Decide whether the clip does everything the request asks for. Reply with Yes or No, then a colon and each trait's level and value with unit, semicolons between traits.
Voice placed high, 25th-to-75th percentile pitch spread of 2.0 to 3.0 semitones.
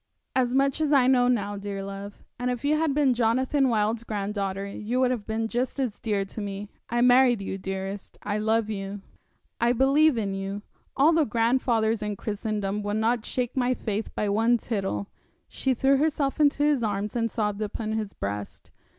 No: high, 225 Hz; average, 3.8 semitones